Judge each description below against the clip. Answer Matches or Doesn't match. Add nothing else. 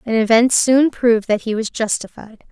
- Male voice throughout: Doesn't match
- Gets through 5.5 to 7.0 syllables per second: Doesn't match